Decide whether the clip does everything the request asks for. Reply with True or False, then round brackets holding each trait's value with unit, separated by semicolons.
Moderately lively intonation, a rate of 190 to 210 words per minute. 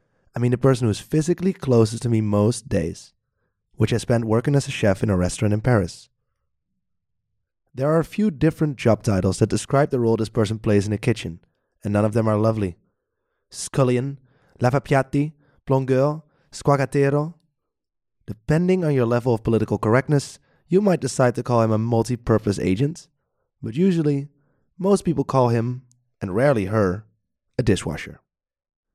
False (4.7 semitones; 160 wpm)